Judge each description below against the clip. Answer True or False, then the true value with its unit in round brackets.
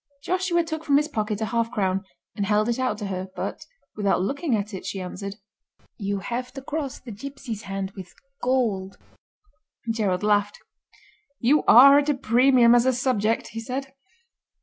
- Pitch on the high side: True (230 Hz)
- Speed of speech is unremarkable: True (170 wpm)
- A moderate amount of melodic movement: True (4.9 semitones)